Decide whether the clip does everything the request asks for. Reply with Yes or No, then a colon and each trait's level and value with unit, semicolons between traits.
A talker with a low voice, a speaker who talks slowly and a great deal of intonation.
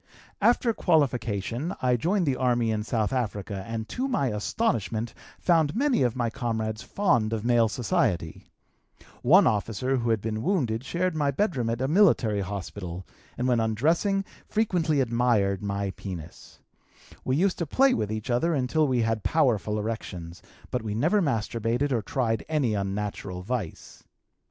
No: low, 120 Hz; average, 155 wpm; wide, 6.0 semitones